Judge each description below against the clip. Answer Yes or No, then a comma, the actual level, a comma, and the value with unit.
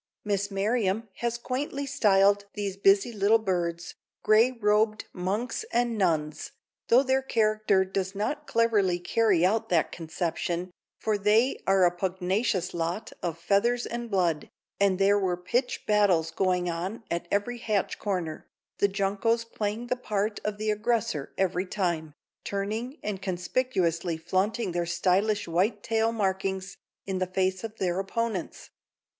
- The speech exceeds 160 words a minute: No, average, 145 wpm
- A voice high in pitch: Yes, high, 200 Hz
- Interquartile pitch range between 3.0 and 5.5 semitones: Yes, average, 3.5 semitones